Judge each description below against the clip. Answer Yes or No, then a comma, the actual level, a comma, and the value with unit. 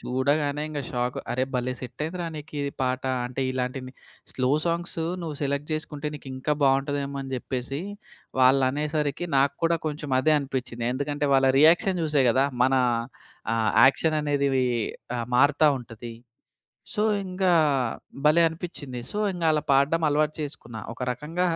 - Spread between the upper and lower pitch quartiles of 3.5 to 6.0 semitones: No, average, 2.9 semitones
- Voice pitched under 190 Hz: Yes, medium, 140 Hz